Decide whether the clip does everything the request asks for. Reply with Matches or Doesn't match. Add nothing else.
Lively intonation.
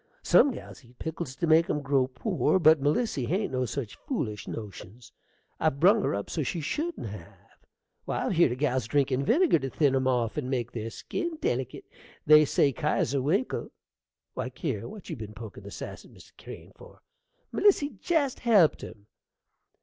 Matches